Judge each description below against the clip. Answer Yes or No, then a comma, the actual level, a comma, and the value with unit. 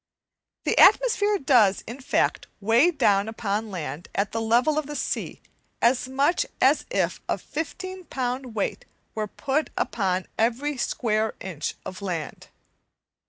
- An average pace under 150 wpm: Yes, average, 140 wpm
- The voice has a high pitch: Yes, high, 235 Hz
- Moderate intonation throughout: No, wide, 6.1 semitones